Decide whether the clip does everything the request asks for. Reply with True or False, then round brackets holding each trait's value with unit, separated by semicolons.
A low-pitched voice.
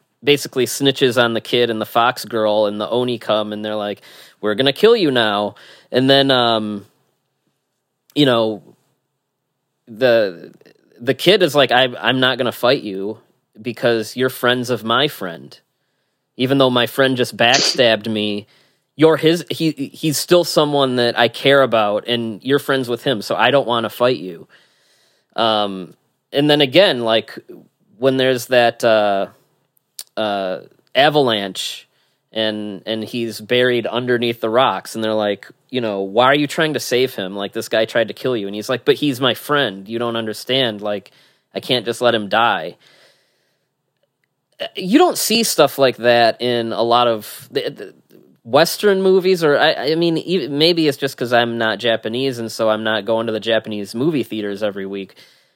True (120 Hz)